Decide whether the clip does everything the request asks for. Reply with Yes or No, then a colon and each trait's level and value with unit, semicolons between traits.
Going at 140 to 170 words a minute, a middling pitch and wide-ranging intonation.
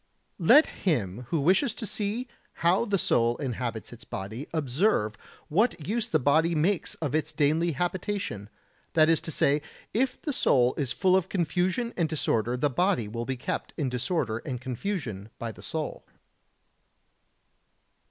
Yes: average, 155 wpm; medium, 155 Hz; wide, 7.3 semitones